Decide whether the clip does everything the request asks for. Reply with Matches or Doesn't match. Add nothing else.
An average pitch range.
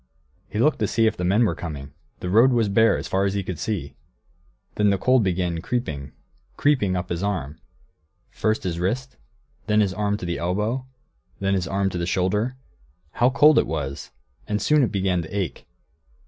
Matches